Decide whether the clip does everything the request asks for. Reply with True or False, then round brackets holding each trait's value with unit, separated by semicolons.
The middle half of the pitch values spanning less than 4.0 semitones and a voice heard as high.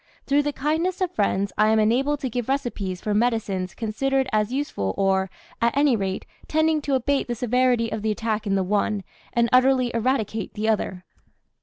False (4.4 semitones; 230 Hz)